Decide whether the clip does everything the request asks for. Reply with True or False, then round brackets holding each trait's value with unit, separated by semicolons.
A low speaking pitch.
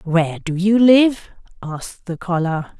False (185 Hz)